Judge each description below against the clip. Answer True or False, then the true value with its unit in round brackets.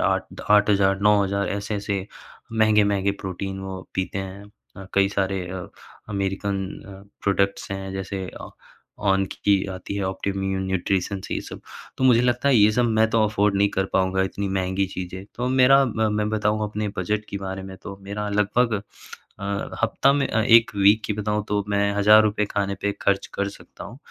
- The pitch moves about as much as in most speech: False (1.6 semitones)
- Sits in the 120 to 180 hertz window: False (100 Hz)